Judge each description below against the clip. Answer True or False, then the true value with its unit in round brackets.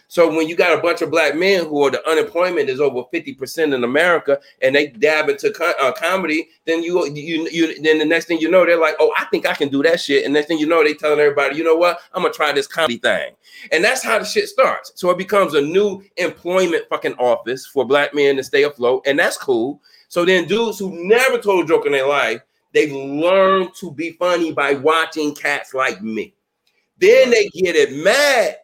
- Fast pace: True (235 wpm)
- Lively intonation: True (6.0 semitones)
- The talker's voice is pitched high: False (170 Hz)